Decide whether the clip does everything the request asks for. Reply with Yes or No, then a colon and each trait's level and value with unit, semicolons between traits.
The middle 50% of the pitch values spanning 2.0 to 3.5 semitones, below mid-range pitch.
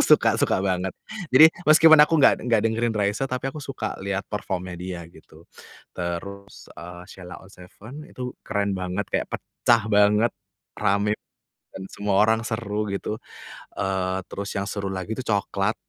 Yes: average, 3.1 semitones; low, 100 Hz